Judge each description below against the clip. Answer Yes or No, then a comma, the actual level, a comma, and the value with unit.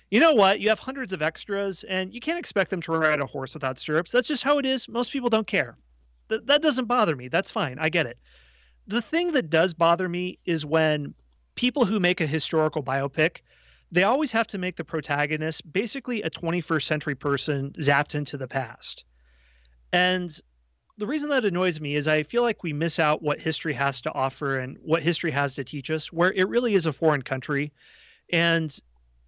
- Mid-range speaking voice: Yes, medium, 160 Hz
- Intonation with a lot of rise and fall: Yes, wide, 5.8 semitones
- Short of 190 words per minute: No, fast, 205 wpm